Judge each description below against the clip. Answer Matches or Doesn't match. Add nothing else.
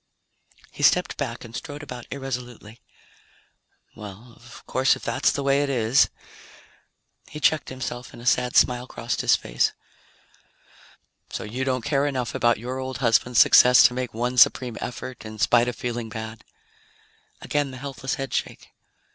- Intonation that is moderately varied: Doesn't match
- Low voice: Matches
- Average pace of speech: Matches